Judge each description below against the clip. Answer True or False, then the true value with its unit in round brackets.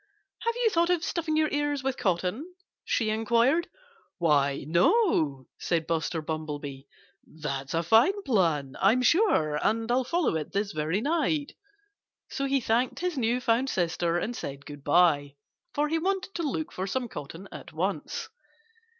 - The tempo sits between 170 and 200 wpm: False (160 wpm)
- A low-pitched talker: False (225 Hz)